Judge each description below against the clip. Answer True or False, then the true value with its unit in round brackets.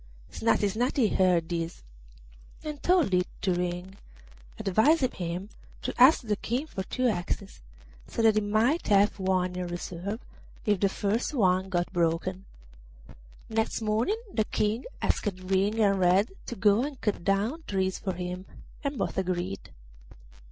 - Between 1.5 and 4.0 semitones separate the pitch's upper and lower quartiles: True (3.6 semitones)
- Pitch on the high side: True (200 Hz)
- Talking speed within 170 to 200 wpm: False (150 wpm)